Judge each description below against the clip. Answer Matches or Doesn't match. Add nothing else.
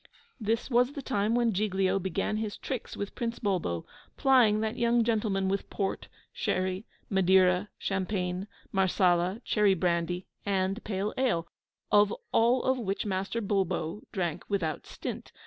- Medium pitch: Doesn't match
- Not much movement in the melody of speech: Doesn't match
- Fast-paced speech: Doesn't match